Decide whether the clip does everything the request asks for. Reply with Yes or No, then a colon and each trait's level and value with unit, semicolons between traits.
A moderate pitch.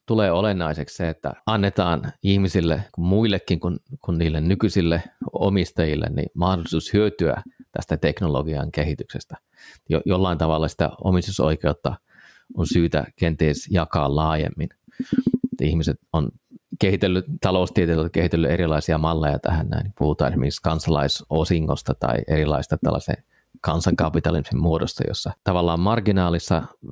No: very low, 85 Hz